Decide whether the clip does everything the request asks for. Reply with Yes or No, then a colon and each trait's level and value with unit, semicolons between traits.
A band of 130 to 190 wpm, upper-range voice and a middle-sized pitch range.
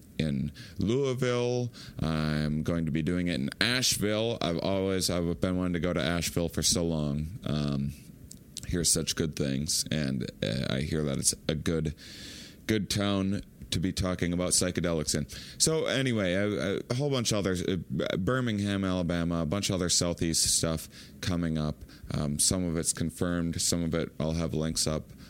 No: average, 170 wpm; very low, 85 Hz; average, 4.0 semitones